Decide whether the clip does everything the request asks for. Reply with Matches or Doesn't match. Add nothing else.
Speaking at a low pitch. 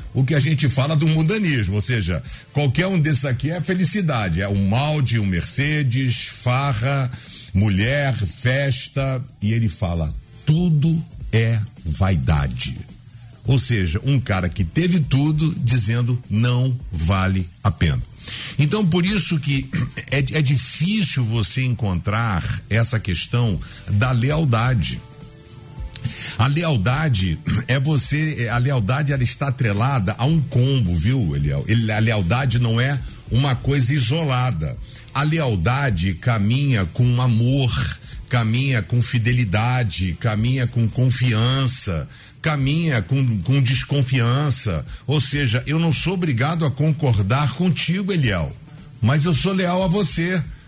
Matches